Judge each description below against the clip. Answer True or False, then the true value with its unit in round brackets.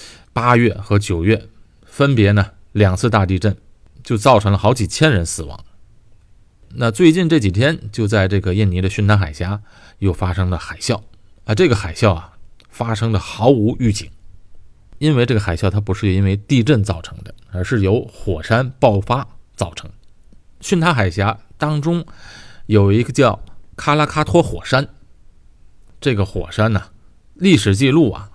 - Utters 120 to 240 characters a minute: True (235 characters per minute)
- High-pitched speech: False (105 Hz)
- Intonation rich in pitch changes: False (4.0 semitones)